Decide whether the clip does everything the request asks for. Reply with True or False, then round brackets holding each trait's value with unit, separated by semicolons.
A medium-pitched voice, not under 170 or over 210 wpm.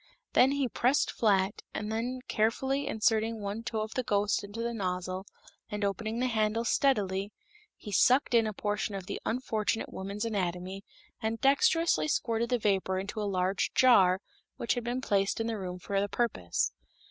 False (215 Hz; 175 wpm)